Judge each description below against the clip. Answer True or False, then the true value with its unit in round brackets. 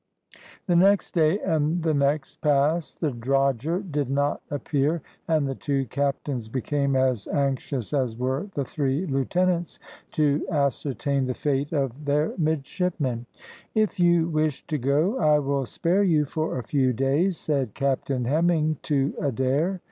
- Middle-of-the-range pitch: True (145 Hz)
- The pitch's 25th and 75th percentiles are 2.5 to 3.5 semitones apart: True (3.0 semitones)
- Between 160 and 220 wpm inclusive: False (150 wpm)